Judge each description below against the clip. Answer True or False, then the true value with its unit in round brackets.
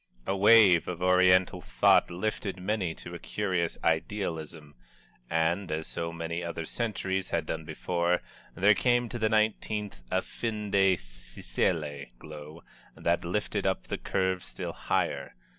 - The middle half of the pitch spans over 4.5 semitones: False (3.7 semitones)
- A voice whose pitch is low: True (90 Hz)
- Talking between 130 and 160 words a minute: True (140 wpm)